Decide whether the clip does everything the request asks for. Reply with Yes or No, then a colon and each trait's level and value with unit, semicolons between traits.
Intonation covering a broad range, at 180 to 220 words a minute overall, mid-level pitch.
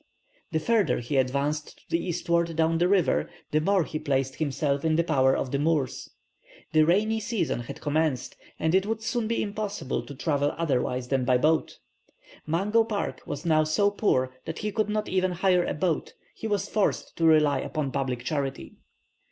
Yes: wide, 5.8 semitones; average, 185 wpm; medium, 160 Hz